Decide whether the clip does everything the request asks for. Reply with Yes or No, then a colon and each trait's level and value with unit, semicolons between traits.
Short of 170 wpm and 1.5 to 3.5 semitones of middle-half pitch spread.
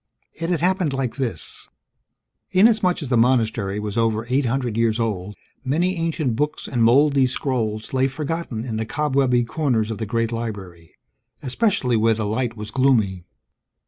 No: average, 160 wpm; average, 4.3 semitones